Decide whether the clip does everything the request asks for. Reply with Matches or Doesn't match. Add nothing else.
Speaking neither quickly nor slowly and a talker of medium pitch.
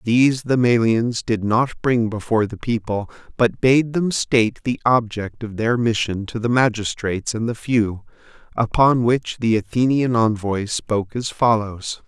Doesn't match